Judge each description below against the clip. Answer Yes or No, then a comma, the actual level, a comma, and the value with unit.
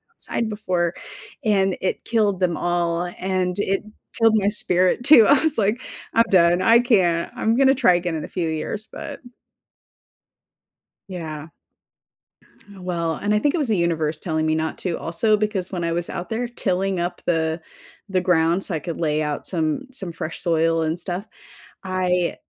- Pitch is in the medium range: Yes, medium, 180 Hz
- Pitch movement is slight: No, average, 3.9 semitones